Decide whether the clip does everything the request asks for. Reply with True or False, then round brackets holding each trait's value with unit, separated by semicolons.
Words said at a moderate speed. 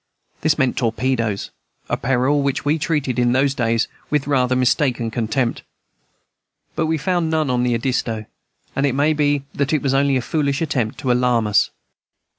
True (175 wpm)